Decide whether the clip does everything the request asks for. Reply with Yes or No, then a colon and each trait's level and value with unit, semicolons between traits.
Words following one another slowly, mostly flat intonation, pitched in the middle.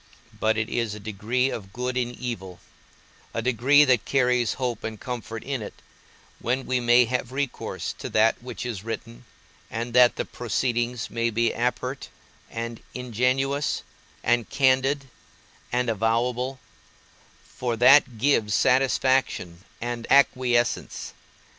No: slow, 130 wpm; narrow, 1.9 semitones; low, 120 Hz